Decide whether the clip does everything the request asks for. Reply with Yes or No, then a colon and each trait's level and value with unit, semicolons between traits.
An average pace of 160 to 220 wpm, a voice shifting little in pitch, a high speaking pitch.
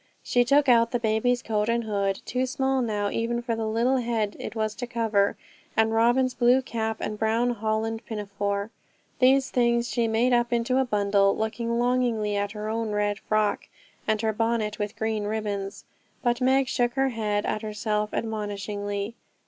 Yes: average, 175 wpm; narrow, 2.3 semitones; high, 225 Hz